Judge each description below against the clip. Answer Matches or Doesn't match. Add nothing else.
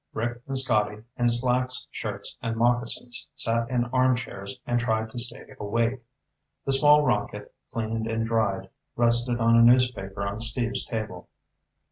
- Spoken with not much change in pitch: Matches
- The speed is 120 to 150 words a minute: Matches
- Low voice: Matches